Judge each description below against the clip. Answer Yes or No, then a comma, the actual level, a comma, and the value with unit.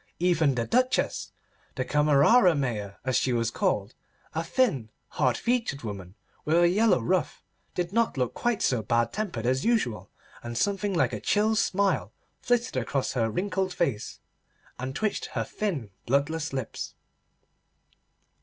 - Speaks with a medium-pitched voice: Yes, medium, 150 Hz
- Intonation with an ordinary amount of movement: No, wide, 9.0 semitones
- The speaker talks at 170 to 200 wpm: No, average, 140 wpm